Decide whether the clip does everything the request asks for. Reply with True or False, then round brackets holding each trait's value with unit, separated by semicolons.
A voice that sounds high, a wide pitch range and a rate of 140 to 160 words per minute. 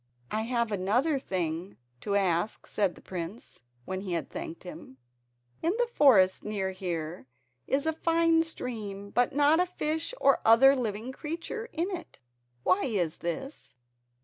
True (220 Hz; 8.4 semitones; 150 wpm)